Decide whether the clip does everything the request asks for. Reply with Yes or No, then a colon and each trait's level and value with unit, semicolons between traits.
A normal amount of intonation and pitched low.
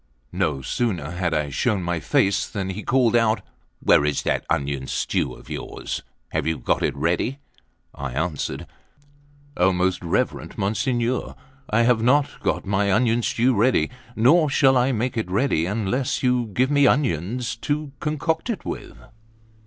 No: wide, 6.4 semitones; low, 110 Hz